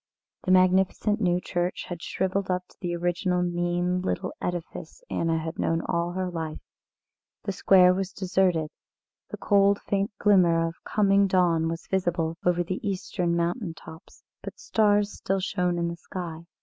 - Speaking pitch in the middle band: Yes, medium, 180 Hz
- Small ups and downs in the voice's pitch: Yes, narrow, 2.0 semitones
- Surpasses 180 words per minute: No, average, 160 wpm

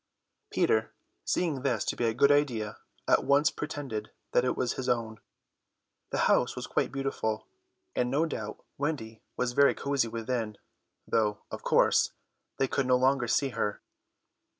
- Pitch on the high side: No, low, 125 Hz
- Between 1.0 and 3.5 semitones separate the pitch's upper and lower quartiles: No, average, 3.9 semitones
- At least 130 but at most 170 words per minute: Yes, average, 155 wpm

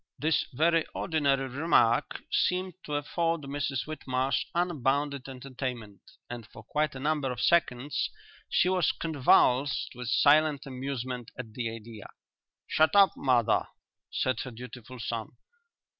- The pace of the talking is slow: Yes, slow, 130 wpm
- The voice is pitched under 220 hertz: Yes, low, 135 Hz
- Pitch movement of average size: Yes, average, 3.7 semitones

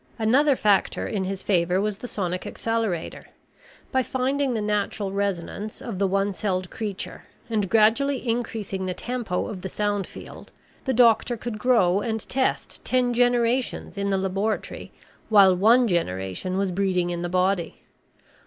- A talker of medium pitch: No, high, 205 Hz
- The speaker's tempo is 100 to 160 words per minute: Yes, average, 155 wpm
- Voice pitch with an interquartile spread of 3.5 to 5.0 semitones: Yes, average, 3.8 semitones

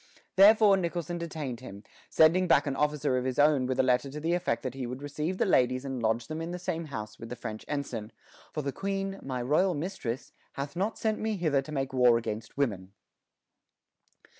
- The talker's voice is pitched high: No, medium, 140 Hz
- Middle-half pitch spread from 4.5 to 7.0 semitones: Yes, wide, 5.4 semitones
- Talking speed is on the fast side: Yes, fast, 210 wpm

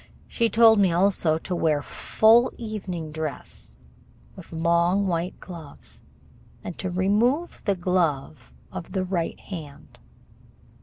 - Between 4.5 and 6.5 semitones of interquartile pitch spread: No, average, 3.6 semitones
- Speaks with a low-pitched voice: No, medium, 180 Hz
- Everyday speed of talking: No, slow, 120 wpm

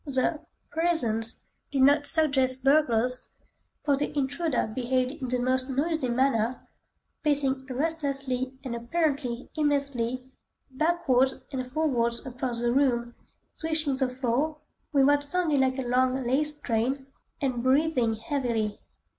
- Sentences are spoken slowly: Yes, slow, 125 wpm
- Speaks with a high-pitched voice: Yes, very high, 265 Hz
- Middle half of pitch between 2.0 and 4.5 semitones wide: Yes, average, 2.7 semitones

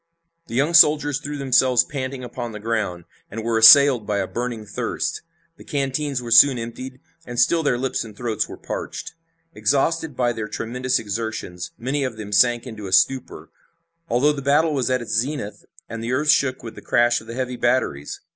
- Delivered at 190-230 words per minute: Yes, average, 195 wpm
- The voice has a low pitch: Yes, low, 125 Hz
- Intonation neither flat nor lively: Yes, average, 3.3 semitones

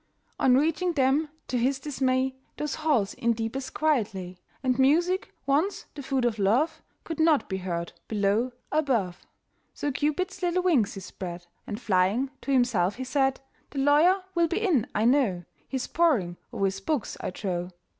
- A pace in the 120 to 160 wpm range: No, average, 170 wpm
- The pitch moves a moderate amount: No, wide, 6.8 semitones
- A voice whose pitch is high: Yes, very high, 260 Hz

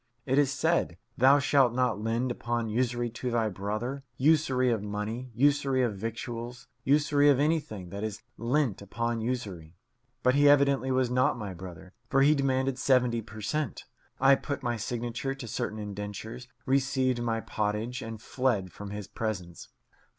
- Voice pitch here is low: Yes, low, 120 Hz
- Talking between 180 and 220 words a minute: No, average, 160 wpm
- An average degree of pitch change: Yes, average, 3.8 semitones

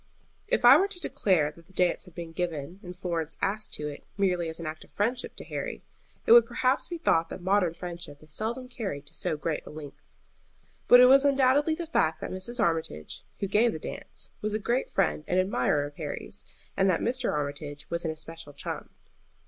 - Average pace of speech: No, fast, 215 wpm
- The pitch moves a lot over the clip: Yes, wide, 6.6 semitones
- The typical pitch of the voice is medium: Yes, medium, 180 Hz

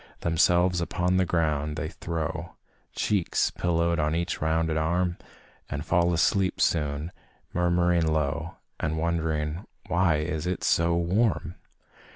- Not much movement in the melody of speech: Yes, narrow, 1.9 semitones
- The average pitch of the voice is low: Yes, very low, 85 Hz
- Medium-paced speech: No, slow, 125 wpm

